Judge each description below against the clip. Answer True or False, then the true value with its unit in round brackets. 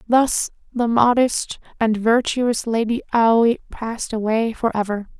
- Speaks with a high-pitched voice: True (230 Hz)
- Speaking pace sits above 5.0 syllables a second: False (4.2 syllables/s)